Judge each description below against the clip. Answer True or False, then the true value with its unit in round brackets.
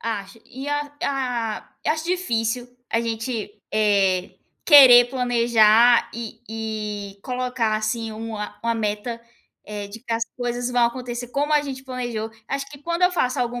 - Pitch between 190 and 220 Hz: False (235 Hz)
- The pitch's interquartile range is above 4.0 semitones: False (2.7 semitones)